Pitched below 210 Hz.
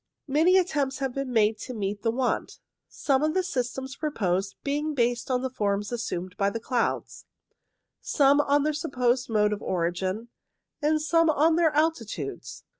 No: very high, 255 Hz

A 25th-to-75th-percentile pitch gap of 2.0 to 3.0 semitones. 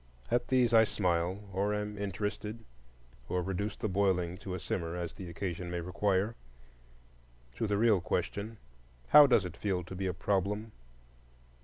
Yes: narrow, 2.6 semitones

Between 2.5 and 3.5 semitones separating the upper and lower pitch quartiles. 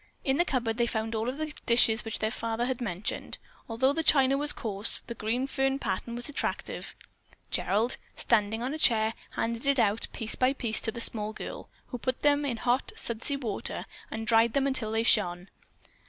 Yes: average, 3.2 semitones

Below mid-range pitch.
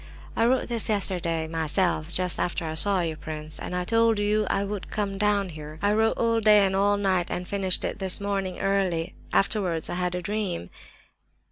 No: high, 195 Hz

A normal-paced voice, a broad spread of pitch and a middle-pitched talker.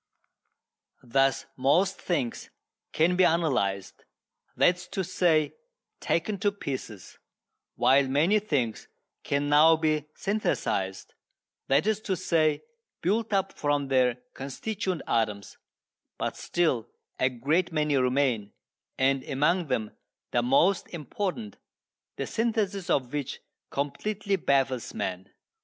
No: slow, 115 wpm; wide, 6.1 semitones; medium, 150 Hz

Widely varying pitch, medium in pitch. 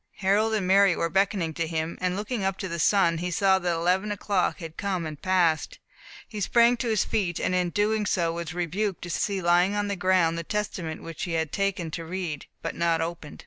No: average, 3.1 semitones; medium, 180 Hz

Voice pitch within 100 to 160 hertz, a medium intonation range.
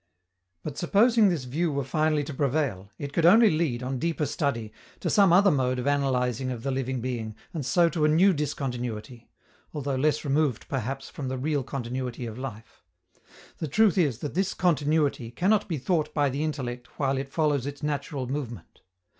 Yes: medium, 140 Hz; average, 3.6 semitones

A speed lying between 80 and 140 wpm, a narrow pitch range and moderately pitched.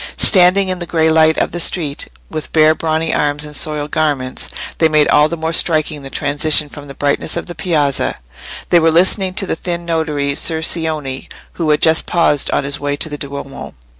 No: fast, 205 wpm; narrow, 2.2 semitones; medium, 155 Hz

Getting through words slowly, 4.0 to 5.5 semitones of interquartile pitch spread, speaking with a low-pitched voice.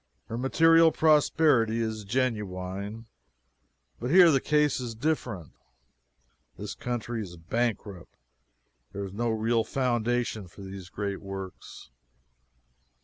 Yes: slow, 110 wpm; average, 4.4 semitones; low, 115 Hz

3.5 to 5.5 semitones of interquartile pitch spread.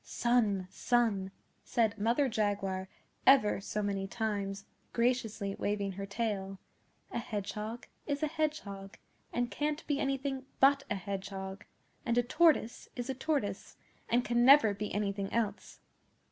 Yes: average, 4.1 semitones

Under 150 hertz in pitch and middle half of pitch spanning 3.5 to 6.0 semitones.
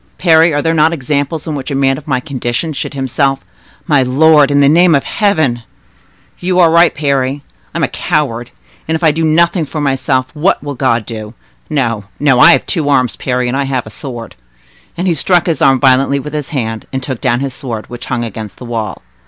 Yes: medium, 140 Hz; average, 3.8 semitones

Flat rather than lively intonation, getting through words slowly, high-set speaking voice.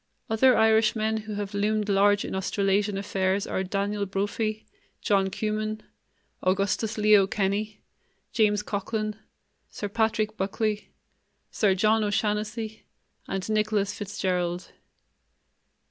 Yes: narrow, 1.5 semitones; slow, 105 wpm; high, 210 Hz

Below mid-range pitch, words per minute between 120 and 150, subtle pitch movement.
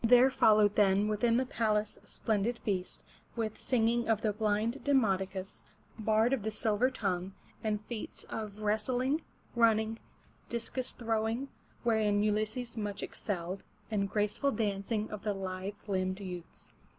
No: high, 215 Hz; average, 145 wpm; narrow, 2.3 semitones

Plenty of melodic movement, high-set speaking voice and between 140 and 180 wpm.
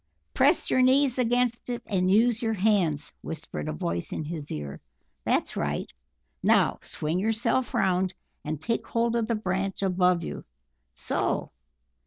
Yes: wide, 6.3 semitones; high, 195 Hz; average, 150 wpm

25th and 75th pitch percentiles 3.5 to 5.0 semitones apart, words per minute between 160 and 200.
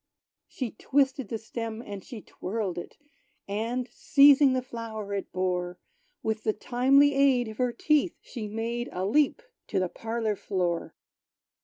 No: average, 4.0 semitones; average, 150 wpm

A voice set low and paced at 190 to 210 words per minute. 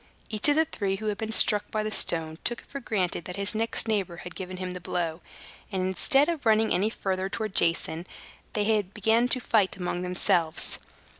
No: high, 200 Hz; fast, 205 wpm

